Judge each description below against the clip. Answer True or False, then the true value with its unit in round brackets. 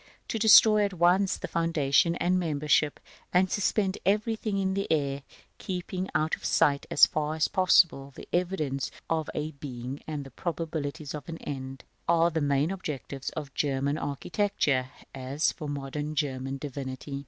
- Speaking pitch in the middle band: True (155 Hz)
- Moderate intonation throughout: True (4.3 semitones)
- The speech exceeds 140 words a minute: True (155 wpm)